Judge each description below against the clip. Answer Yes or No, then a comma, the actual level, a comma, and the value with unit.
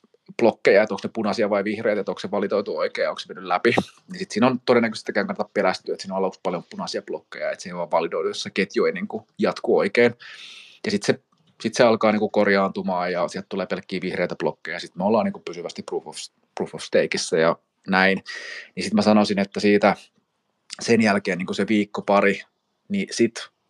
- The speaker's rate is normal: No, fast, 215 wpm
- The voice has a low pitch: Yes, low, 125 Hz